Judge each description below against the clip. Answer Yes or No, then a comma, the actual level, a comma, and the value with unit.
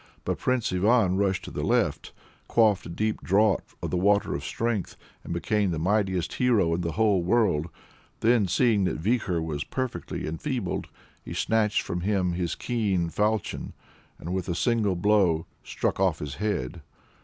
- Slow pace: No, average, 165 wpm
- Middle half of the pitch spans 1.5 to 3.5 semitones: No, average, 3.9 semitones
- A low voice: Yes, very low, 95 Hz